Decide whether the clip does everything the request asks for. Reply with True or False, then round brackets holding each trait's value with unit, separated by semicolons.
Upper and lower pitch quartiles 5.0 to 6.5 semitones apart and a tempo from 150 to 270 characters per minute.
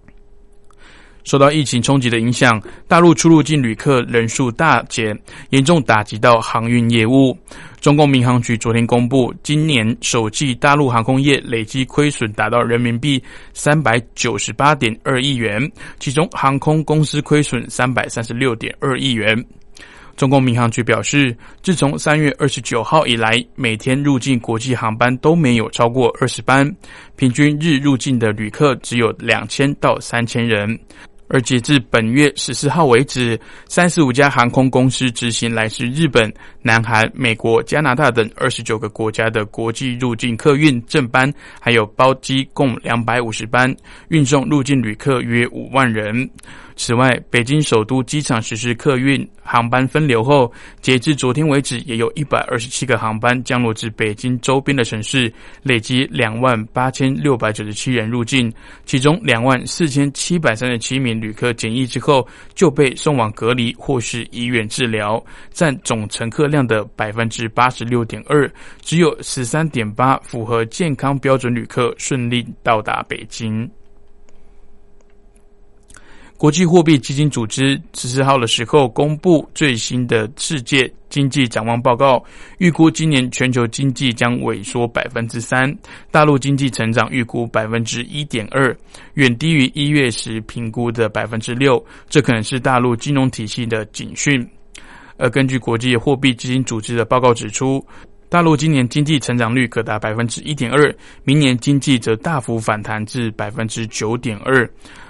False (3.3 semitones; 255 characters per minute)